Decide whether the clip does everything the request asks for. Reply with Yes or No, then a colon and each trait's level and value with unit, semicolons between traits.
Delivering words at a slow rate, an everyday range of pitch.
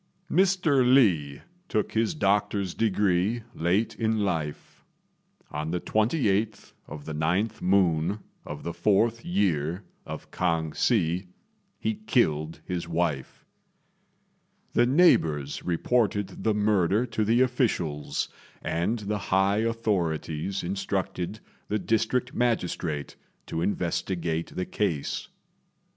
Yes: slow, 110 wpm; average, 5.0 semitones